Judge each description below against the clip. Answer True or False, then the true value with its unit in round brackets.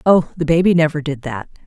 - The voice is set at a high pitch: False (155 Hz)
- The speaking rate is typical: False (215 wpm)